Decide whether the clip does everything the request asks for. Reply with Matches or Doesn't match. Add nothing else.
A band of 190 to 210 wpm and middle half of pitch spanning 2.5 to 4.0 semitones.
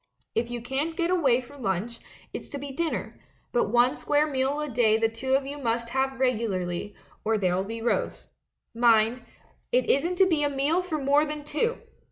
Doesn't match